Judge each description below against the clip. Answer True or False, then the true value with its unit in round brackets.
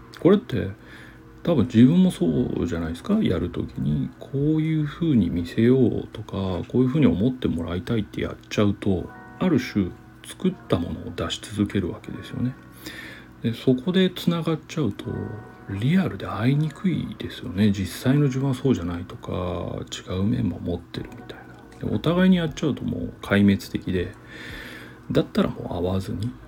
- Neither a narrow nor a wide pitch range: False (6.8 semitones)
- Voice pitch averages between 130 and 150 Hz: False (110 Hz)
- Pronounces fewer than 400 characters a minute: True (355 characters per minute)